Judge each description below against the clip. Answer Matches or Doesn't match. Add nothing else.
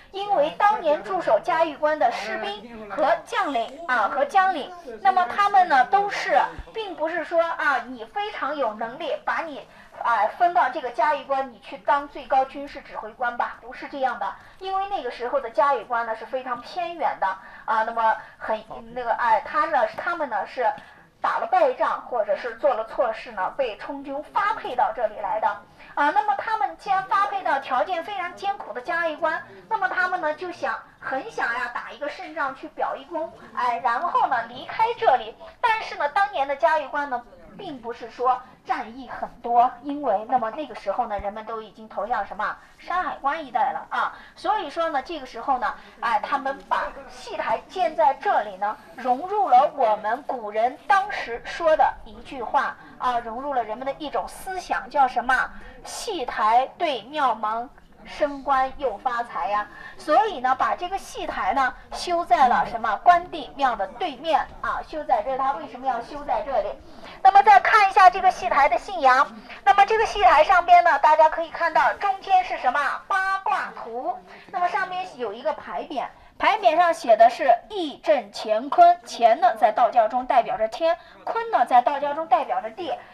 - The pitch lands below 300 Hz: Doesn't match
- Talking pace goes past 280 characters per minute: Doesn't match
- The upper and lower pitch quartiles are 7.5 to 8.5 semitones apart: Doesn't match